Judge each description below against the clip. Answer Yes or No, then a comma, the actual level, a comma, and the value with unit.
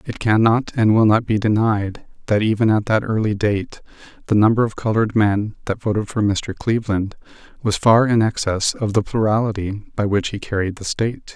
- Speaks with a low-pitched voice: Yes, low, 105 Hz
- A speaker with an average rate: Yes, average, 190 wpm